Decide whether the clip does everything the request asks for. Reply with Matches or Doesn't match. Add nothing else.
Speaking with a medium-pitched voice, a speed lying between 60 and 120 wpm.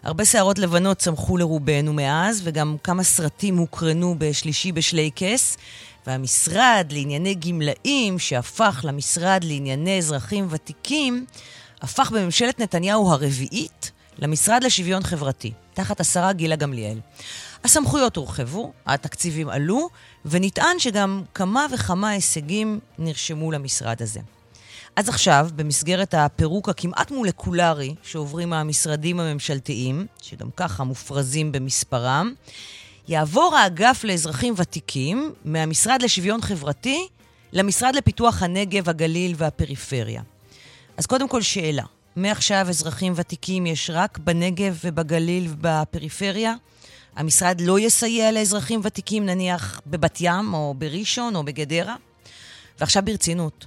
Matches